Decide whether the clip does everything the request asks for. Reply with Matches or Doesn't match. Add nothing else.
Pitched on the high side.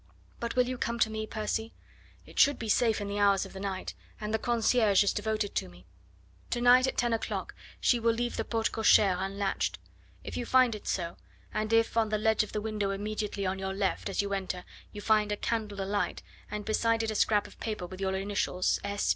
Matches